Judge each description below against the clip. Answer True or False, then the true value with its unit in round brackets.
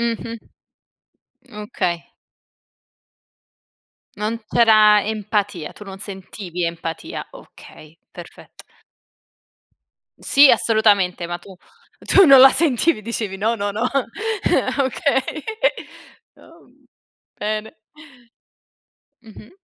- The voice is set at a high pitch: True (215 Hz)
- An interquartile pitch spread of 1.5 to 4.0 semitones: False (4.4 semitones)